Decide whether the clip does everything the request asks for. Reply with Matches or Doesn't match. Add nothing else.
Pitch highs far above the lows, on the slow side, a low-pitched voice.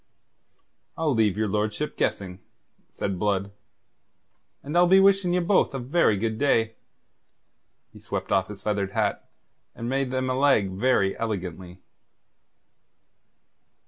Matches